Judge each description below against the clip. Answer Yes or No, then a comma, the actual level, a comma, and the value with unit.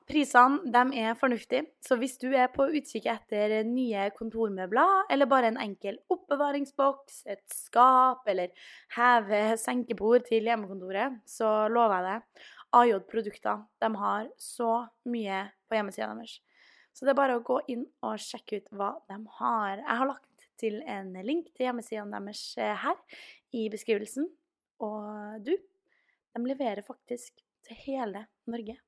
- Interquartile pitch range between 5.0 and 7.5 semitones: No, average, 3.7 semitones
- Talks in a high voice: Yes, high, 235 Hz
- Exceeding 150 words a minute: No, average, 145 wpm